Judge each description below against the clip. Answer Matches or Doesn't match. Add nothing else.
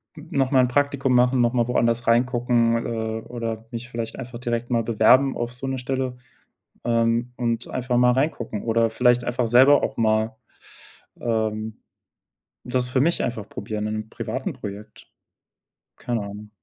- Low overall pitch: Matches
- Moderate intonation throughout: Doesn't match